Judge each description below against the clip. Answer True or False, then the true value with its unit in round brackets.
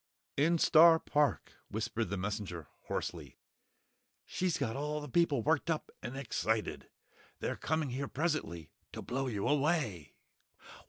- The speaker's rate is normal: False (130 wpm)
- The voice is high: False (135 Hz)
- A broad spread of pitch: True (6.2 semitones)